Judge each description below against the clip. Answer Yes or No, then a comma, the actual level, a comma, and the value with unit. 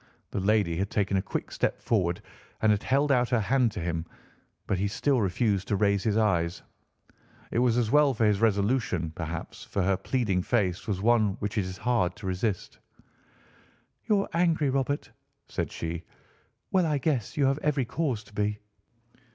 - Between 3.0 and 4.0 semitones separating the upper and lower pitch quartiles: No, average, 5.1 semitones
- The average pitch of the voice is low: Yes, low, 105 Hz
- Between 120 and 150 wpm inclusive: No, average, 180 wpm